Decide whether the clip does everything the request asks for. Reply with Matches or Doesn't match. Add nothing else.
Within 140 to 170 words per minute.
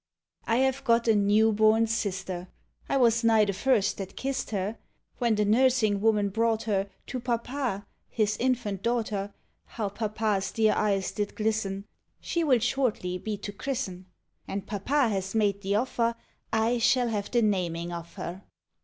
Matches